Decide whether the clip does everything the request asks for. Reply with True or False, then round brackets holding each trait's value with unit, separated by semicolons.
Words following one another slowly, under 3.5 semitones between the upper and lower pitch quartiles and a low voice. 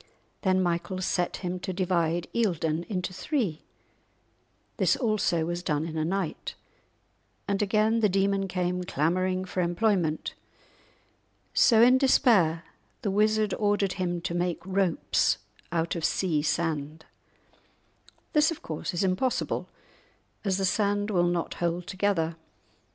False (130 wpm; 3.1 semitones; 185 Hz)